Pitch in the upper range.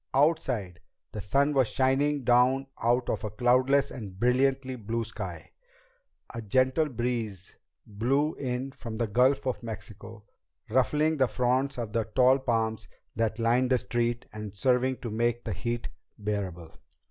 No: low, 120 Hz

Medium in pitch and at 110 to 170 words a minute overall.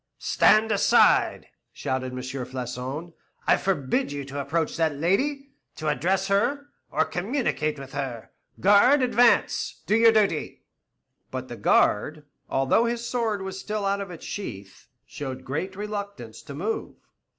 Yes: medium, 180 Hz; average, 140 wpm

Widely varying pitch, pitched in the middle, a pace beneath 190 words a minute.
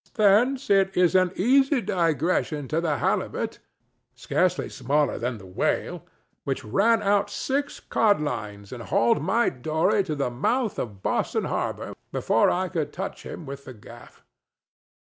Yes: wide, 7.3 semitones; medium, 170 Hz; average, 140 wpm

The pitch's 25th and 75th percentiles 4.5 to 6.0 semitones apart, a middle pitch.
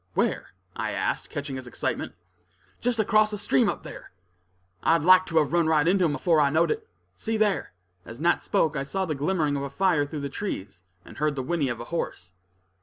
Yes: average, 4.8 semitones; medium, 160 Hz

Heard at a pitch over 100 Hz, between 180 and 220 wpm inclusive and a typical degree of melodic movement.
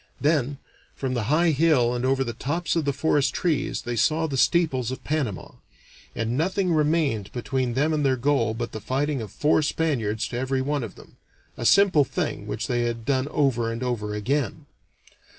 Yes: low, 135 Hz; average, 190 wpm; average, 4.2 semitones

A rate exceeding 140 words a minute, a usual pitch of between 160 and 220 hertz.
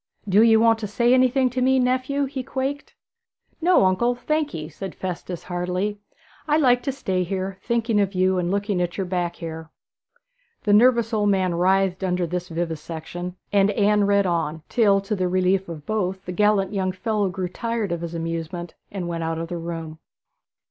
Yes: average, 185 wpm; high, 190 Hz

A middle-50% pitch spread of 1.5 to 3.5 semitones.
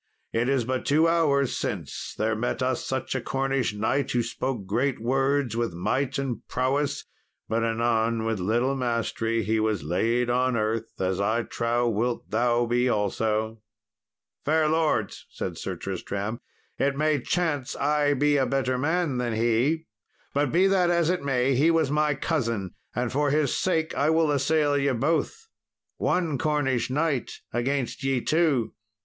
No: average, 4.1 semitones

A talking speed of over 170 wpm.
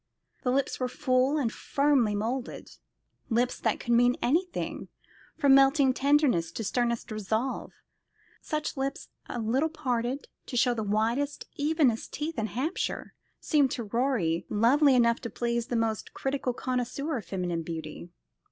No: average, 145 wpm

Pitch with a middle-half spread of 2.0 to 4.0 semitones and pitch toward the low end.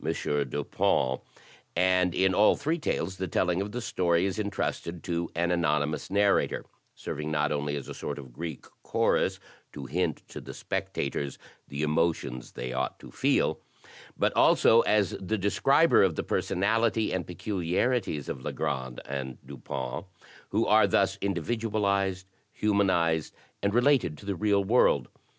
No: average, 5.3 semitones; very low, 90 Hz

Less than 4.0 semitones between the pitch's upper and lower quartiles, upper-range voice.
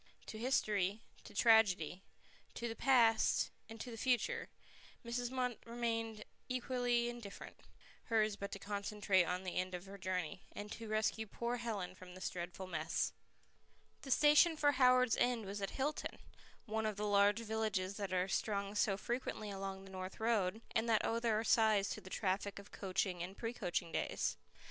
Yes: average, 3.4 semitones; high, 215 Hz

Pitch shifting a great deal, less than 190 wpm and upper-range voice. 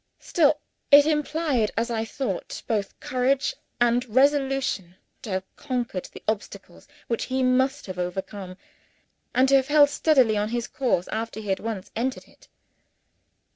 No: average, 4.4 semitones; average, 150 wpm; high, 245 Hz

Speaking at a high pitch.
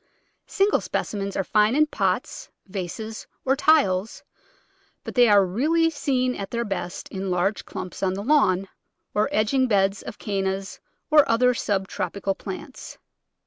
Yes: high, 210 Hz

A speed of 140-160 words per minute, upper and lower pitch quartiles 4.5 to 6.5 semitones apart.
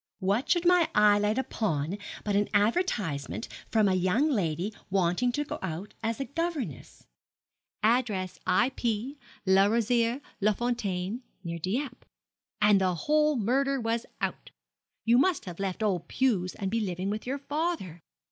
Yes: average, 150 wpm; wide, 5.5 semitones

